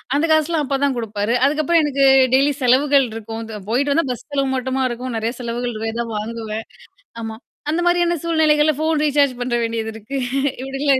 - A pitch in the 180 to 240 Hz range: No, very high, 265 Hz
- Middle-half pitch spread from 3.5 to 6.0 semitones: Yes, average, 4.2 semitones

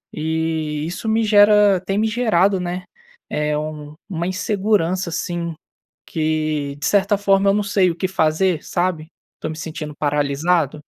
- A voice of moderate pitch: Yes, medium, 175 Hz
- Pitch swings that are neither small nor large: Yes, average, 4.1 semitones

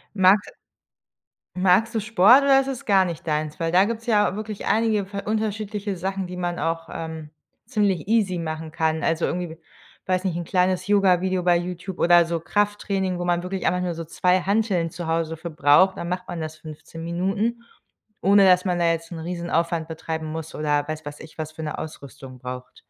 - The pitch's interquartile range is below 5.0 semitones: Yes, average, 3.3 semitones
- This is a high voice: No, medium, 175 Hz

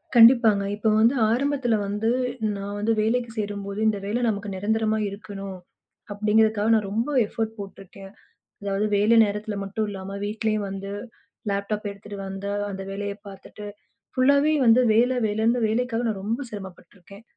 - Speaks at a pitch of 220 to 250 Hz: No, high, 210 Hz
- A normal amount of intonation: No, narrow, 2.1 semitones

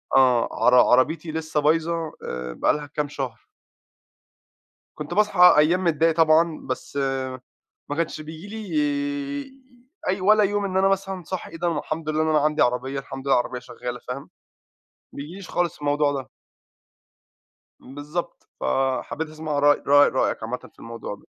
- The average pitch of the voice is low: No, medium, 155 Hz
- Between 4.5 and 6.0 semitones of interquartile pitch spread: No, average, 3.9 semitones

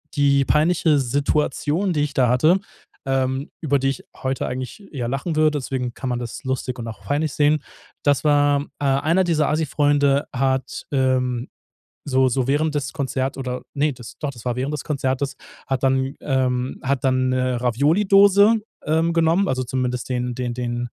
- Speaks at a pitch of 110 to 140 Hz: Yes, low, 135 Hz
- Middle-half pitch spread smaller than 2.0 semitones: No, average, 2.8 semitones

